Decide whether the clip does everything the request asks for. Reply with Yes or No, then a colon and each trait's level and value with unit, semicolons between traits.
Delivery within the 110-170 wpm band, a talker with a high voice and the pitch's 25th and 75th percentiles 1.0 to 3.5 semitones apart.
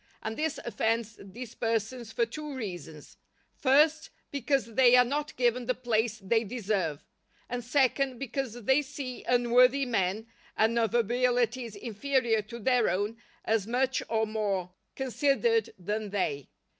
Yes: average, 140 wpm; high, 235 Hz; average, 3.1 semitones